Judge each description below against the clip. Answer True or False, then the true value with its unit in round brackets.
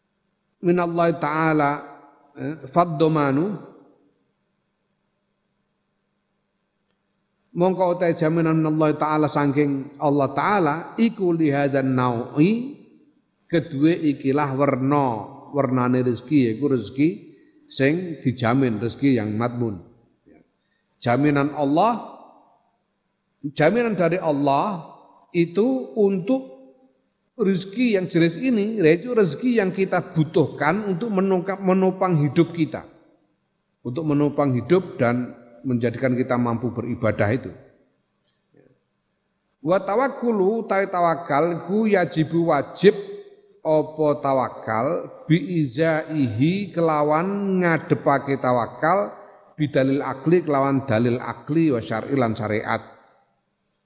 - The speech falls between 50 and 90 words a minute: True (85 wpm)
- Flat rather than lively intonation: False (5.2 semitones)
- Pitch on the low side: False (155 Hz)